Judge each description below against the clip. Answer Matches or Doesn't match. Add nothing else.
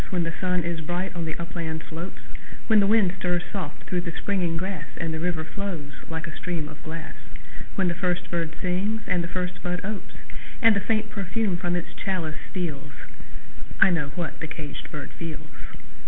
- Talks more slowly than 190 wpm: Doesn't match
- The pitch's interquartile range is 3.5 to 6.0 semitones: Doesn't match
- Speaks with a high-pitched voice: Doesn't match